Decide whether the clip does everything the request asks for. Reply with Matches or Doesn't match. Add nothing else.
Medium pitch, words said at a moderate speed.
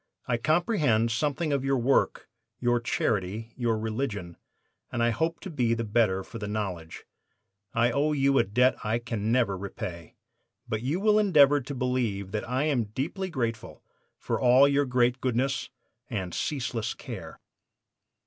Doesn't match